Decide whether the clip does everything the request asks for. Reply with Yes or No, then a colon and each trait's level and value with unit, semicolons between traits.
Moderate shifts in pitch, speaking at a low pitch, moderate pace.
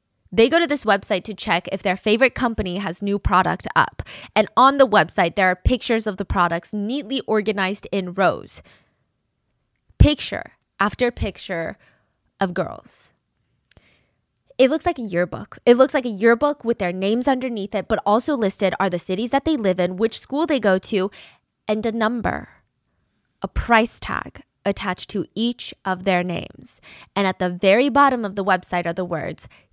No: average, 4.2 semitones; high, 210 Hz; average, 175 wpm